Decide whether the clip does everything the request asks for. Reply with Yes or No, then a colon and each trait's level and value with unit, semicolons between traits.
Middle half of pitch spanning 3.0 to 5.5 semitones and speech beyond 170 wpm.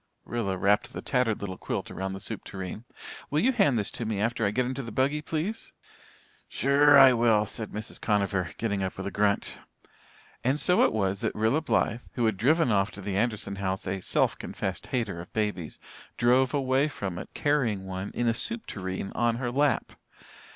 Yes: average, 4.9 semitones; average, 195 wpm